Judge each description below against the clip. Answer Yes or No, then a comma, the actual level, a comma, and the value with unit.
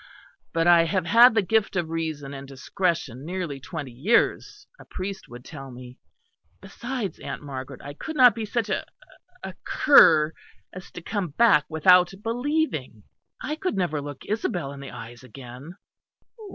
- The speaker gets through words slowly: No, average, 160 wpm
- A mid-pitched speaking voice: Yes, medium, 165 Hz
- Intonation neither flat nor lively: No, wide, 7.4 semitones